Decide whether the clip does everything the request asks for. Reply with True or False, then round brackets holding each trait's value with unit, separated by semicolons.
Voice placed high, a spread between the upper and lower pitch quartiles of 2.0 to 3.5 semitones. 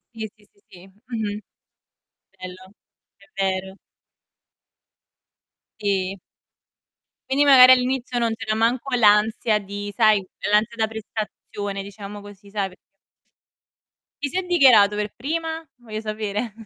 True (215 Hz; 2.9 semitones)